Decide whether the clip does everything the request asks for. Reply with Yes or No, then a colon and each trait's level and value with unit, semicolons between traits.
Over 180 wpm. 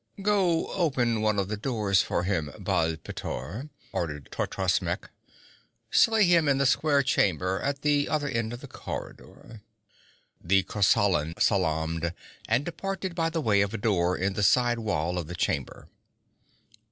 No: average, 155 wpm